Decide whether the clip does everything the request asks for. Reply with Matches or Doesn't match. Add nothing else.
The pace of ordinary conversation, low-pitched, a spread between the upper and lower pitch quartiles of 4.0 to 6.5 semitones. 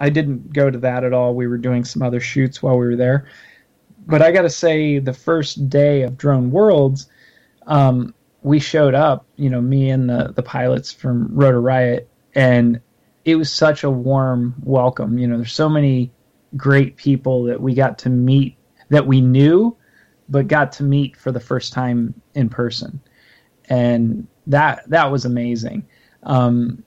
Doesn't match